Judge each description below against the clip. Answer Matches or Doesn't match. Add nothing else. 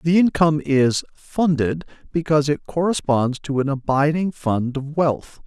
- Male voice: Matches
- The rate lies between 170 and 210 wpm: Doesn't match